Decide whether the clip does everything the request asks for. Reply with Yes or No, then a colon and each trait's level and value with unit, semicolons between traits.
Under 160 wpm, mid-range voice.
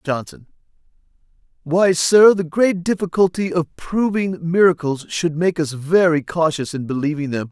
Yes: slow, 135 wpm; medium, 170 Hz